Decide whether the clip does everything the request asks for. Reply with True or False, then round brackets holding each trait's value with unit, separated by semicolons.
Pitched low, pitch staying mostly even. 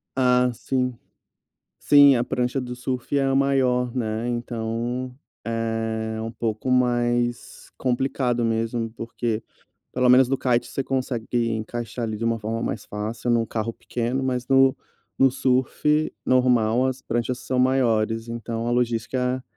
True (120 Hz; 1.9 semitones)